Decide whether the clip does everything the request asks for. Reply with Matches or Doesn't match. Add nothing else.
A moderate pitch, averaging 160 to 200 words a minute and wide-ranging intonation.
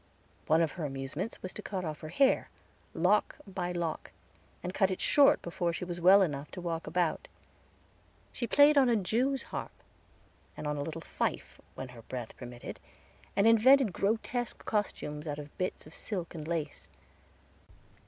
Matches